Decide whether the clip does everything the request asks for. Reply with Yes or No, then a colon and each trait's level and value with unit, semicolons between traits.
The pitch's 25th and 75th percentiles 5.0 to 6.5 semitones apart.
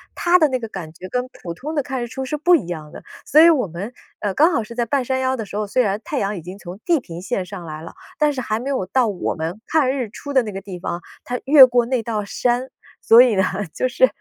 Yes: wide, 5.5 semitones